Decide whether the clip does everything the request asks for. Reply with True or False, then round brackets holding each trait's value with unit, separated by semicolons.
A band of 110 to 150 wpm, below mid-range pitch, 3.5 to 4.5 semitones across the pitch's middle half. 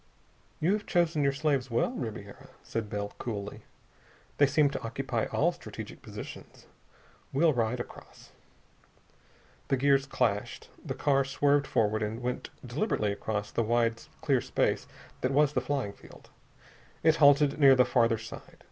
True (145 wpm; 130 Hz; 4.1 semitones)